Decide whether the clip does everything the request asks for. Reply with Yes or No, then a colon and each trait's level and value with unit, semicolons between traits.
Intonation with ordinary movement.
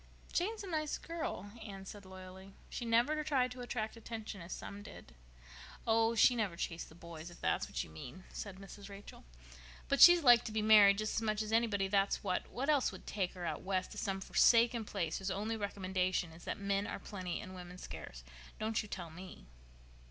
Yes: average, 3.5 semitones